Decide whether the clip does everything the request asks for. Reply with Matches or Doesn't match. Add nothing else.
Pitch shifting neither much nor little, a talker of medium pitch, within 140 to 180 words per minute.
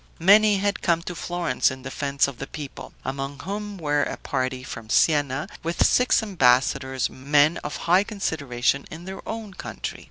Doesn't match